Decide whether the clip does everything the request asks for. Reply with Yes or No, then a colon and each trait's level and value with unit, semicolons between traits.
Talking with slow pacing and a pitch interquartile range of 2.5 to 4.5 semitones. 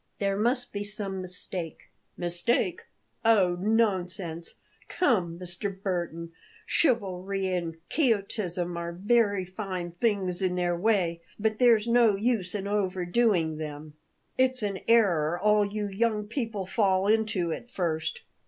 Yes: slow, 125 wpm; average, 3.7 semitones